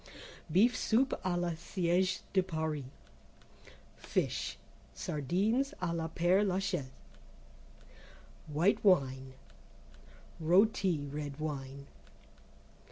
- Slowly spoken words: Yes, slow, 85 wpm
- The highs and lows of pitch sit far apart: No, average, 4.2 semitones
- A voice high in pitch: No, medium, 175 Hz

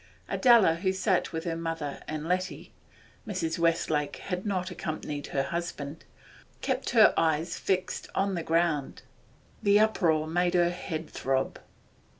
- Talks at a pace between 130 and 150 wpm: Yes, average, 140 wpm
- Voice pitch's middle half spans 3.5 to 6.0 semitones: No, average, 3.0 semitones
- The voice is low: No, medium, 170 Hz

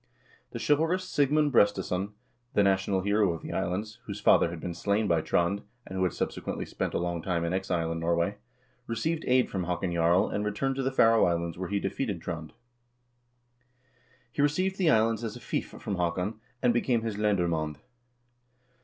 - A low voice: Yes, low, 100 Hz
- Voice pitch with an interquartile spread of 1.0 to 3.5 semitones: No, average, 4.8 semitones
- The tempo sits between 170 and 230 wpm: Yes, average, 180 wpm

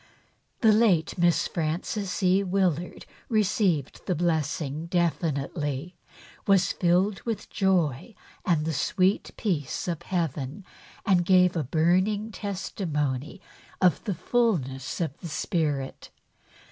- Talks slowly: Yes, slow, 110 wpm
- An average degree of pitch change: Yes, average, 3.9 semitones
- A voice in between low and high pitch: Yes, medium, 175 Hz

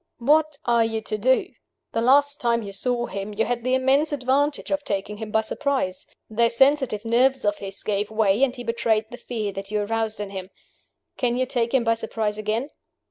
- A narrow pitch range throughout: No, average, 3.5 semitones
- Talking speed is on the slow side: No, fast, 205 wpm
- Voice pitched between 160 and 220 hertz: No, high, 230 Hz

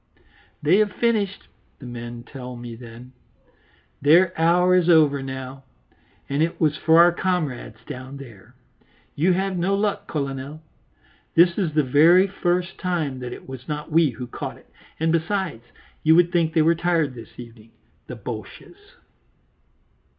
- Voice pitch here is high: No, medium, 155 Hz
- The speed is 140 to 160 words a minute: Yes, average, 155 wpm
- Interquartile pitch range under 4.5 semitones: No, average, 5.1 semitones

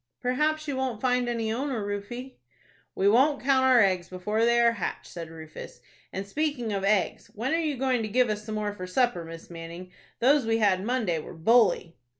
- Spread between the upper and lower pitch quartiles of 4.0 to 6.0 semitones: Yes, average, 4.9 semitones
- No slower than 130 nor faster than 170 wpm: No, average, 200 wpm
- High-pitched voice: Yes, high, 225 Hz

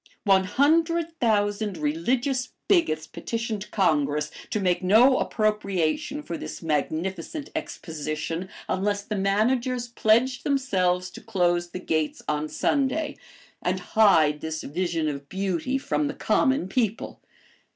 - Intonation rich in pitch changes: Yes, wide, 7.2 semitones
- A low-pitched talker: No, high, 200 Hz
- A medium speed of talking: No, slow, 120 wpm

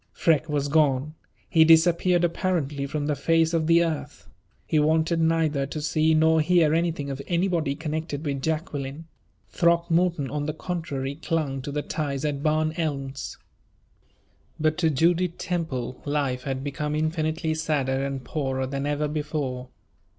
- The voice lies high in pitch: No, medium, 155 Hz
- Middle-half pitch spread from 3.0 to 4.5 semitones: No, narrow, 2.6 semitones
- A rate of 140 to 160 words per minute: Yes, average, 150 wpm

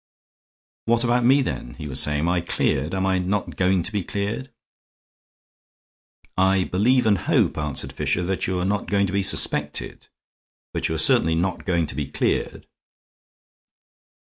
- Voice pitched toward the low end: Yes, very low, 95 Hz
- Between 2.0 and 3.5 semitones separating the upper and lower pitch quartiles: No, average, 3.9 semitones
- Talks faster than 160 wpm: Yes, average, 170 wpm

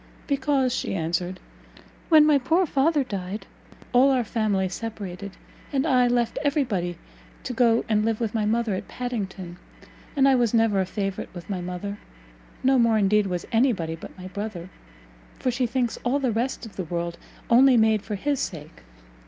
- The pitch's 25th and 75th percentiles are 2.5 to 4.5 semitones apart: No, average, 5.0 semitones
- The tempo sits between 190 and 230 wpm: No, average, 180 wpm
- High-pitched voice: Yes, high, 225 Hz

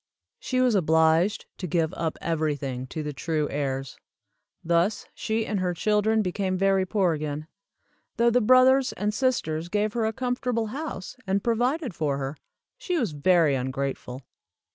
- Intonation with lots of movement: Yes, wide, 6.3 semitones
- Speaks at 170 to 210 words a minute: No, average, 155 wpm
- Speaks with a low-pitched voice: No, medium, 185 Hz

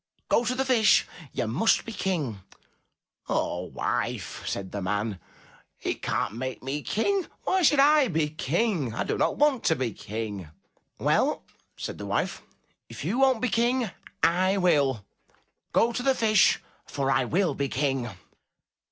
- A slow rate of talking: No, average, 160 wpm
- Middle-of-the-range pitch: Yes, medium, 170 Hz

